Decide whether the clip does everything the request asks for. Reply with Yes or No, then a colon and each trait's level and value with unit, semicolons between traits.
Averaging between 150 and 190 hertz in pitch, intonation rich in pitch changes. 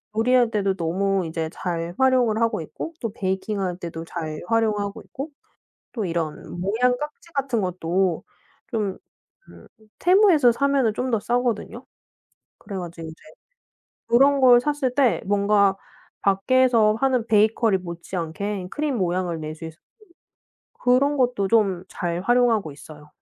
No: high, 210 Hz; wide, 5.7 semitones